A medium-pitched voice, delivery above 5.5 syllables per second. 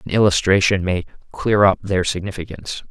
No: very low, 95 Hz; 5.7 syllables/s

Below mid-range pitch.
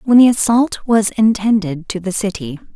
No: high, 215 Hz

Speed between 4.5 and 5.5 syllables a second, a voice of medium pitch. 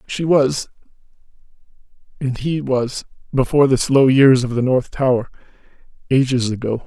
No: 4.8 syllables/s; low, 130 Hz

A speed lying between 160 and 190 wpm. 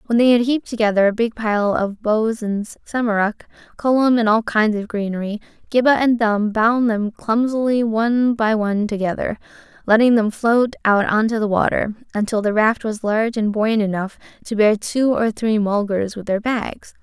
Yes: average, 185 wpm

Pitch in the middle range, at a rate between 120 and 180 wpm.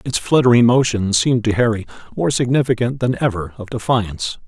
No: low, 120 Hz; average, 160 wpm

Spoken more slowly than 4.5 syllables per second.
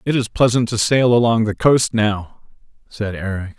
No: 4.7 syllables/s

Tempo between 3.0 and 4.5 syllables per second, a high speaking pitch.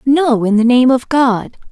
Yes: 4.0 syllables/s; very high, 250 Hz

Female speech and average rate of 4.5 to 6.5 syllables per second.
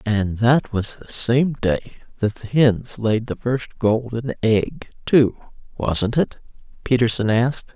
No: female; 3.8 syllables/s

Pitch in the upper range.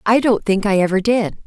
Yes: high, 205 Hz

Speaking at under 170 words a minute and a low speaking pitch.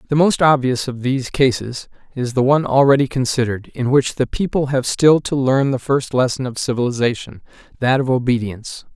No: average, 180 wpm; low, 130 Hz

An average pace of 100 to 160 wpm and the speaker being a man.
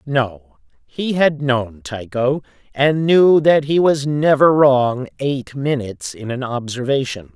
Yes: average, 140 wpm; male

